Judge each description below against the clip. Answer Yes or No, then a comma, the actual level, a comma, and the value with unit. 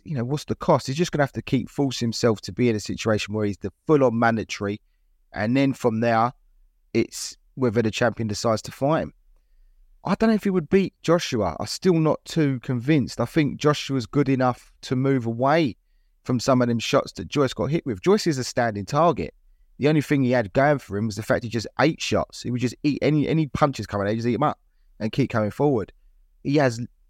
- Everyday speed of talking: No, fast, 235 wpm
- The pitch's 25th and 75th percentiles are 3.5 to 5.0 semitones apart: Yes, average, 4.5 semitones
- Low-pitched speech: Yes, low, 125 Hz